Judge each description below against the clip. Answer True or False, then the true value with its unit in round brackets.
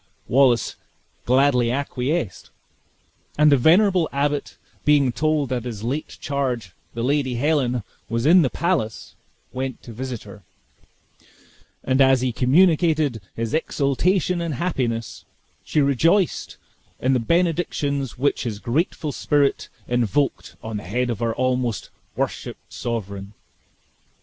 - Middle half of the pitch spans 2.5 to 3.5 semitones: False (4.1 semitones)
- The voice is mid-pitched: False (130 Hz)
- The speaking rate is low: True (125 wpm)